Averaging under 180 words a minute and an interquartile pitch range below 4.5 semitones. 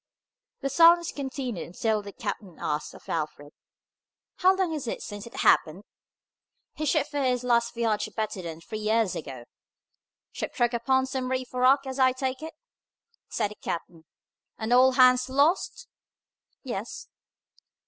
Yes: average, 155 wpm; average, 4.1 semitones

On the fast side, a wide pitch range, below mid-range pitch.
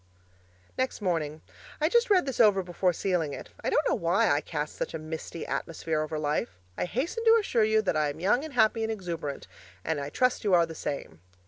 No: fast, 220 wpm; wide, 8.0 semitones; medium, 185 Hz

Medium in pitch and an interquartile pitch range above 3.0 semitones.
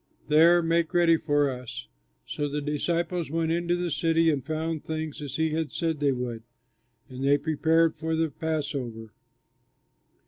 No: medium, 160 Hz; narrow, 2.4 semitones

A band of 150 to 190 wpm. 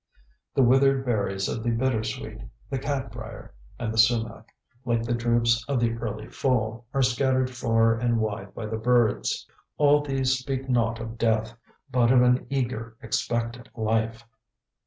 Yes: average, 155 wpm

